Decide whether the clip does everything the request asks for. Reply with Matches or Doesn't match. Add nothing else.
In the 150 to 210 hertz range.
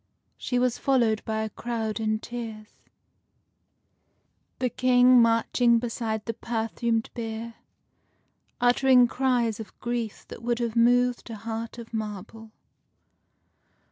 Doesn't match